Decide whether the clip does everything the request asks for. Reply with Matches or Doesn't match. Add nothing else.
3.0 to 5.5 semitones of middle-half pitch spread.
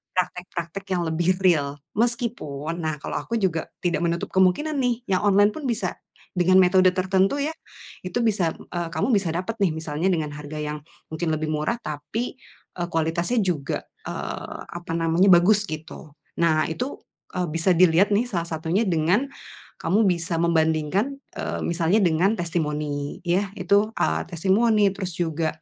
Matches